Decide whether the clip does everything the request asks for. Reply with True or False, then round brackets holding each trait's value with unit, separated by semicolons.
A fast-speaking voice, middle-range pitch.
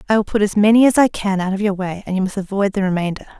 False (320 wpm; 200 Hz)